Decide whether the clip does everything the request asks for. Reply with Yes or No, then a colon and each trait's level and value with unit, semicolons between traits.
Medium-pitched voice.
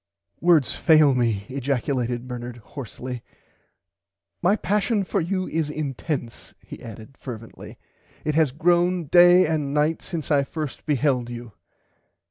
Yes: medium, 145 Hz